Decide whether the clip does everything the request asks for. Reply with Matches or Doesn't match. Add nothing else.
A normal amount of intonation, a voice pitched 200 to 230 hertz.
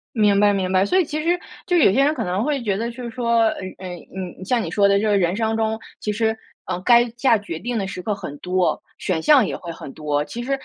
Matches